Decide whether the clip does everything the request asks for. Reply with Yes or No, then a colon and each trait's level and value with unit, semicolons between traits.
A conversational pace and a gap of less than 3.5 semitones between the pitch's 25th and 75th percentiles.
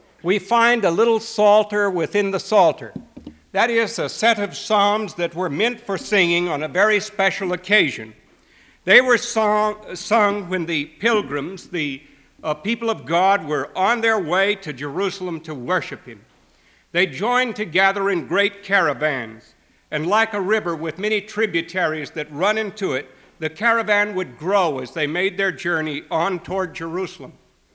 No: average, 160 wpm; average, 4.4 semitones